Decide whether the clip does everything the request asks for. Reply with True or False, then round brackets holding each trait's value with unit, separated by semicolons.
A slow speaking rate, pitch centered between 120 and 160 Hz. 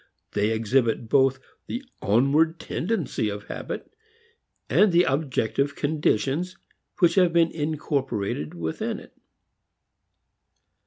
True (100 wpm; 140 Hz)